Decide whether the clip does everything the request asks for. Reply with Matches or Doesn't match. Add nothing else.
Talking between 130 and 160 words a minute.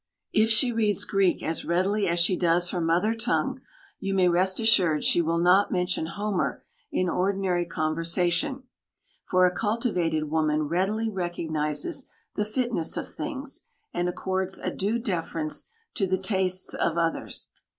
Matches